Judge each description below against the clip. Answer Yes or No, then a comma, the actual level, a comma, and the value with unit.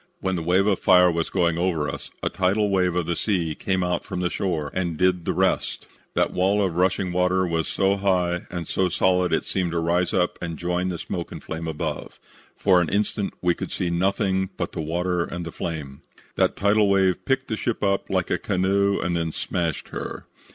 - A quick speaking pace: Yes, fast, 220 wpm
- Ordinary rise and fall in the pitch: No, narrow, 2.0 semitones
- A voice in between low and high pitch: No, very low, 90 Hz